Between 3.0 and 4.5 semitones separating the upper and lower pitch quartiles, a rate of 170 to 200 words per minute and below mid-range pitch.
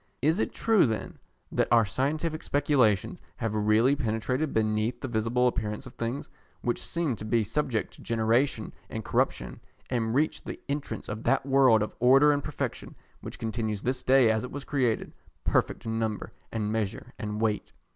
Yes: average, 3.8 semitones; average, 175 wpm; low, 120 Hz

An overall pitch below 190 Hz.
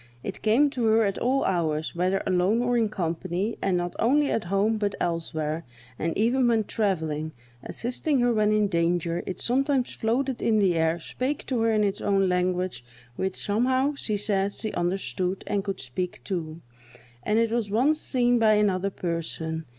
No: high, 200 Hz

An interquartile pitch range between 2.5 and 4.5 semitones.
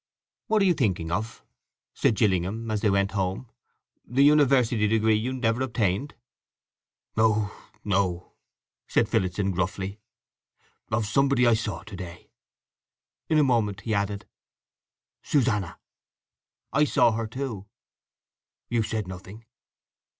Yes: average, 3.7 semitones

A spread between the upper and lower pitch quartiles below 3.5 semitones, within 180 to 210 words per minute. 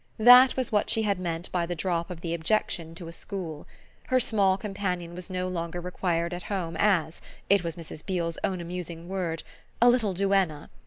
Yes: average, 2.9 semitones; average, 195 wpm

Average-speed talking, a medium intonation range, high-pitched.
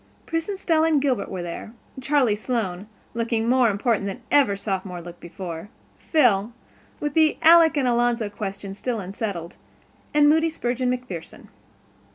No: average, 155 wpm; wide, 6.5 semitones; high, 230 Hz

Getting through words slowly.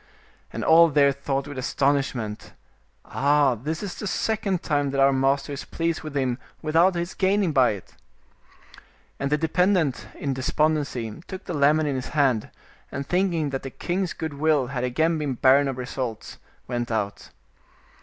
No: average, 175 wpm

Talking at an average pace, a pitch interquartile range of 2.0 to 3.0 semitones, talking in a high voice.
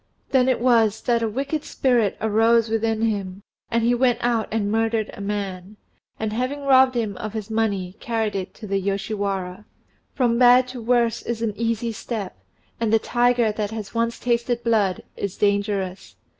Yes: average, 175 wpm; narrow, 2.6 semitones; high, 225 Hz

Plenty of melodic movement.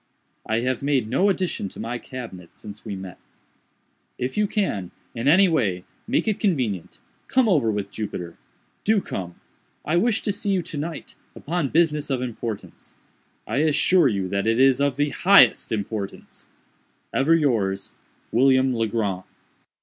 Yes: wide, 7.9 semitones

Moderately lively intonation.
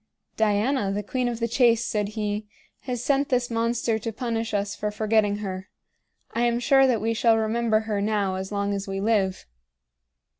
No: narrow, 2.3 semitones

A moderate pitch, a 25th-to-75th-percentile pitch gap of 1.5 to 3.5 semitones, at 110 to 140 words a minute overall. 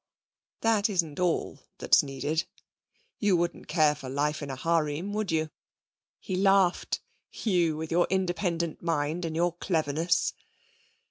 Yes: medium, 170 Hz; average, 3.0 semitones; slow, 135 wpm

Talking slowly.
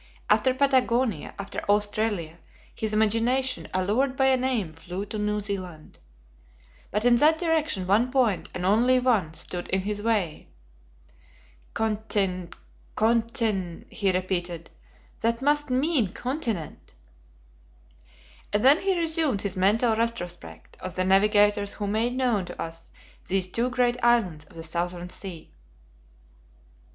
Yes: slow, 130 wpm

